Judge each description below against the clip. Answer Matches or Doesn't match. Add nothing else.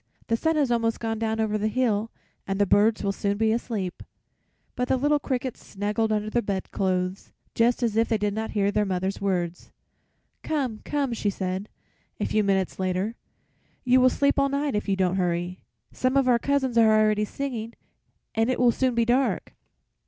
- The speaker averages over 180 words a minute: Matches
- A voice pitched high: Matches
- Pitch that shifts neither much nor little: Matches